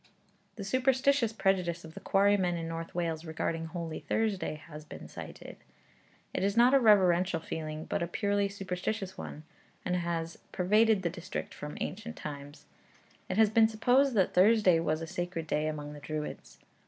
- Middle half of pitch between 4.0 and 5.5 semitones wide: Yes, average, 4.4 semitones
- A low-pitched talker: No, medium, 180 Hz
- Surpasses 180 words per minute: No, average, 165 wpm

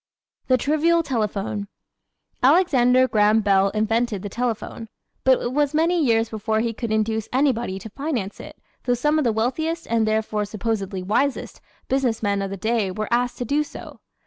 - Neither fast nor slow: Yes, average, 175 wpm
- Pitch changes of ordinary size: Yes, average, 3.7 semitones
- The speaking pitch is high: Yes, high, 230 Hz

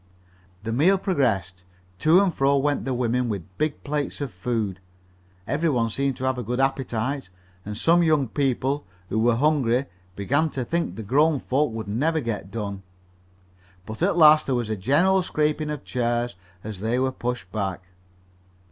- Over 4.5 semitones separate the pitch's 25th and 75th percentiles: Yes, average, 5.1 semitones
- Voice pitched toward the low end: Yes, low, 130 Hz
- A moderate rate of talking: Yes, average, 175 wpm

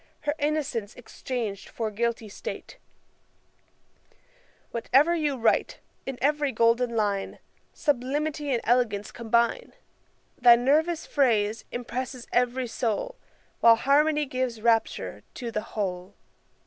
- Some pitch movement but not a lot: Yes, average, 3.9 semitones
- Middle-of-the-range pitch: No, high, 245 Hz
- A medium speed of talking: No, slow, 110 wpm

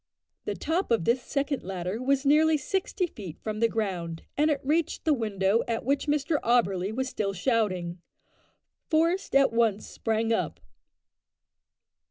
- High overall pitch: Yes, high, 235 Hz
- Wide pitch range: Yes, wide, 6.4 semitones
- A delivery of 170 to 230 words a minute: No, average, 150 wpm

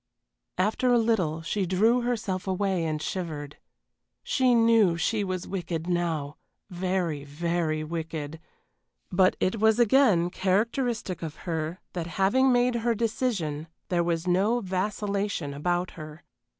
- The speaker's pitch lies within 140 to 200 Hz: Yes, medium, 185 Hz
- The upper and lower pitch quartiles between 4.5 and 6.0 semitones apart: Yes, average, 5.0 semitones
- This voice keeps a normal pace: No, slow, 130 wpm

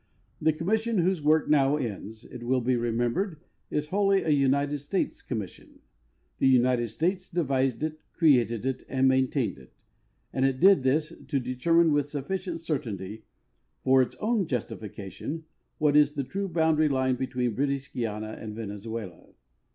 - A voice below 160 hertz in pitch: Yes, low, 135 Hz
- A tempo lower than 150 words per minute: No, average, 160 wpm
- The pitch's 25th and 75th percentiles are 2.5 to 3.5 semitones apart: No, average, 4.7 semitones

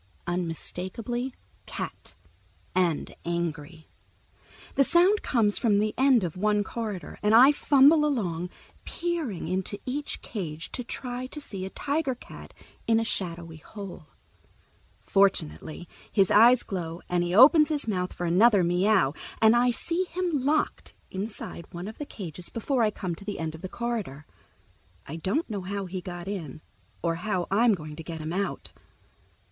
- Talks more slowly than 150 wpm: No, average, 160 wpm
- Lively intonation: Yes, wide, 5.9 semitones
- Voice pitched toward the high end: Yes, high, 200 Hz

